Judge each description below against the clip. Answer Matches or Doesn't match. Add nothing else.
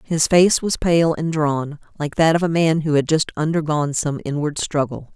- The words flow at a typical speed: Doesn't match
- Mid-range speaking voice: Matches